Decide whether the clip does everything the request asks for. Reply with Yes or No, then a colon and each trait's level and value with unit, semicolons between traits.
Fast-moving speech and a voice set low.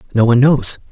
No: average, 195 wpm; low, 125 Hz